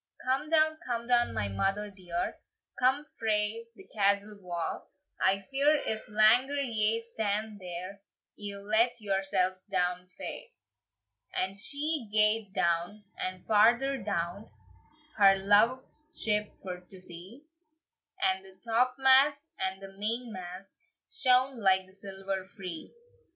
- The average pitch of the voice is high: Yes, high, 210 Hz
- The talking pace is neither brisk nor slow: No, slow, 125 wpm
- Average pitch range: Yes, average, 4.2 semitones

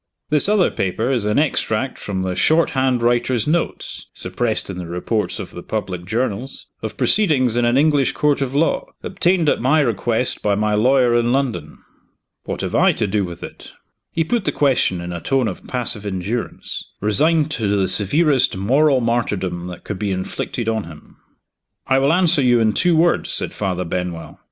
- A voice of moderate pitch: No, low, 120 Hz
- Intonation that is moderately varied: No, wide, 6.0 semitones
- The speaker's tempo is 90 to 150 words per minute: No, average, 185 wpm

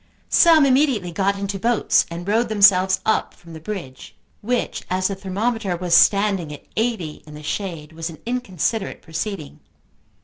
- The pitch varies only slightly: No, average, 4.5 semitones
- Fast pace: No, average, 160 wpm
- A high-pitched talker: Yes, high, 195 Hz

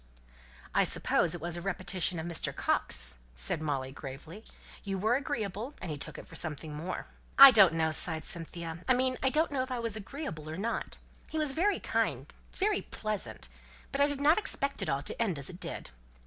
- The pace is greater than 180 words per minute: Yes, fast, 205 wpm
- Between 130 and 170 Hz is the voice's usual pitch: No, high, 190 Hz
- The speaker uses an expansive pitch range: Yes, wide, 8.4 semitones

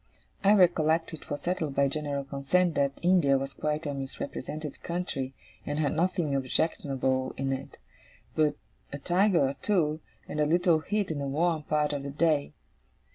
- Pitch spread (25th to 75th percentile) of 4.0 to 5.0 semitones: No, average, 3.5 semitones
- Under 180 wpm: Yes, average, 170 wpm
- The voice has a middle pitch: Yes, medium, 150 Hz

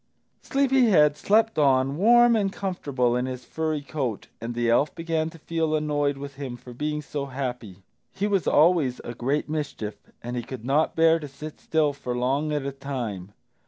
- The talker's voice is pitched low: No, medium, 145 Hz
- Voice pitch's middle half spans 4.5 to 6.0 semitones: No, average, 4.1 semitones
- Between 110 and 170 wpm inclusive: No, average, 190 wpm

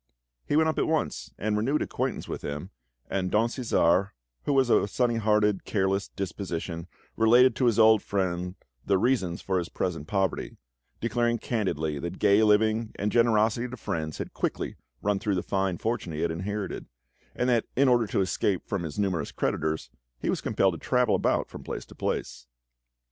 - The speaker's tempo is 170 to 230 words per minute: Yes, average, 185 wpm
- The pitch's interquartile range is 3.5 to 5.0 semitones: Yes, average, 4.3 semitones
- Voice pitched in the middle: No, low, 100 Hz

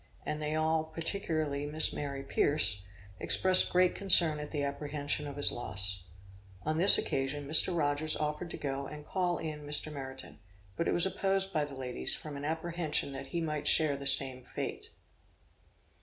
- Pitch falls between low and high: Yes, medium, 150 Hz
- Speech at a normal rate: Yes, average, 170 wpm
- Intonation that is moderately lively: No, narrow, 2.3 semitones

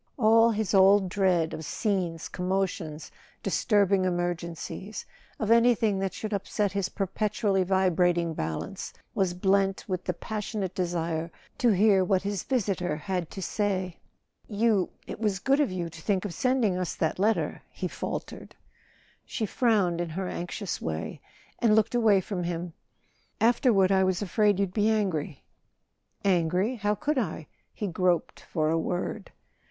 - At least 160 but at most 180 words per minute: No, average, 145 wpm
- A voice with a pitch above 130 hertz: Yes, high, 190 Hz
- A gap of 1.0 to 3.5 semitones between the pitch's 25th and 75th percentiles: Yes, average, 3.1 semitones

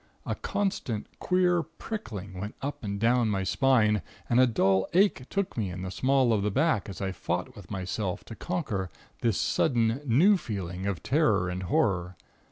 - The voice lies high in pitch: No, low, 110 Hz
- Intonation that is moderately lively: No, wide, 6.3 semitones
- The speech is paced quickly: No, average, 175 wpm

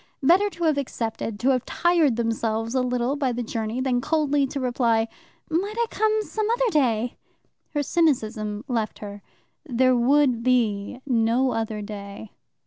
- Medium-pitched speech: No, very high, 250 Hz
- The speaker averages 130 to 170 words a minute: Yes, average, 155 wpm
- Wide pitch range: No, average, 4.5 semitones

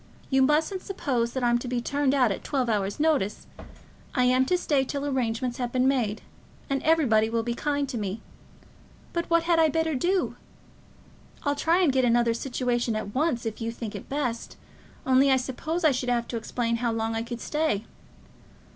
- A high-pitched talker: Yes, very high, 255 Hz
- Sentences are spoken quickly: No, average, 195 wpm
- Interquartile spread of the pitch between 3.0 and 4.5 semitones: Yes, average, 3.8 semitones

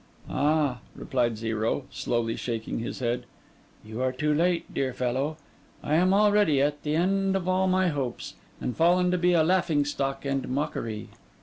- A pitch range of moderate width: No, wide, 6.0 semitones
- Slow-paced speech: No, average, 170 wpm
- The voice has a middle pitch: Yes, medium, 145 Hz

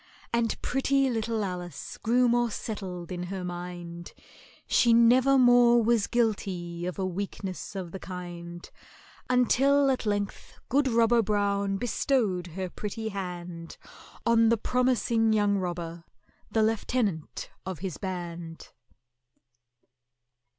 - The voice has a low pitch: No, high, 205 Hz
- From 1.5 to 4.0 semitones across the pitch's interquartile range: No, average, 4.8 semitones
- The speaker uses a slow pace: Yes, slow, 120 wpm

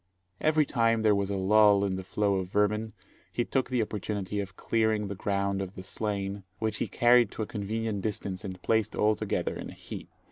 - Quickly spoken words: Yes, fast, 210 wpm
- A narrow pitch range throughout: Yes, narrow, 2.0 semitones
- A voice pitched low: Yes, low, 105 Hz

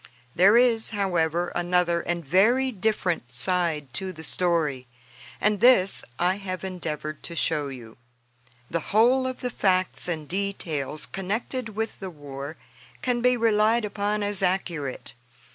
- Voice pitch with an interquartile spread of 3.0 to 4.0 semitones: No, average, 4.7 semitones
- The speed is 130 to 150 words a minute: Yes, average, 140 wpm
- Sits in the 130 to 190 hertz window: Yes, medium, 185 Hz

